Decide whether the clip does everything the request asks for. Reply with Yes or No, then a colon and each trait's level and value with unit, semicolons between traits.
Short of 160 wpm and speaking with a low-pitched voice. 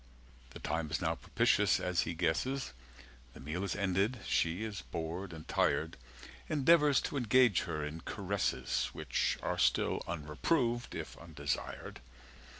Yes: average, 140 wpm; very low, 90 Hz